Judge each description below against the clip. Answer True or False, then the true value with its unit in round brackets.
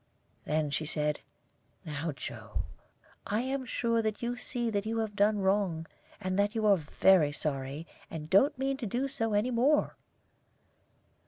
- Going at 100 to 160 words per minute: True (155 wpm)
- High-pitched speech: True (205 Hz)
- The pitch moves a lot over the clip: True (6.6 semitones)